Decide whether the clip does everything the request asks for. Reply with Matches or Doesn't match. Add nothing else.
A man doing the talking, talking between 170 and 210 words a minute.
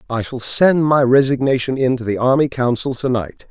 Matches